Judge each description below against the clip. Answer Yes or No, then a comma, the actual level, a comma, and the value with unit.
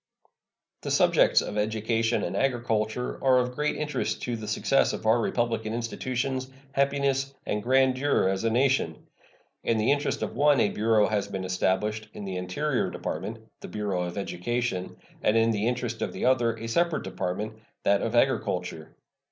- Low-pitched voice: Yes, low, 115 Hz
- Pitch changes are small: No, average, 3.7 semitones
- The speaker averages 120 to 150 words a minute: No, average, 170 wpm